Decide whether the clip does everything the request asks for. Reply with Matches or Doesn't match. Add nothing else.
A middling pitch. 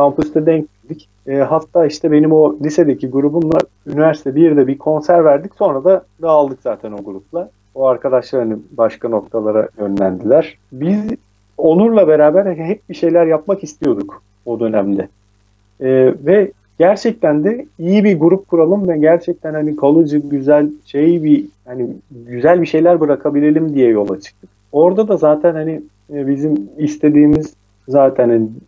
Matches